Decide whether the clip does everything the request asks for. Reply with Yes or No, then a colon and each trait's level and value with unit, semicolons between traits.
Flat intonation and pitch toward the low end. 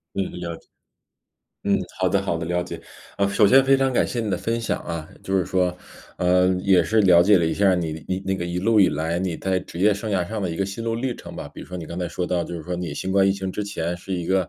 Yes: narrow, 2.3 semitones; very low, 95 Hz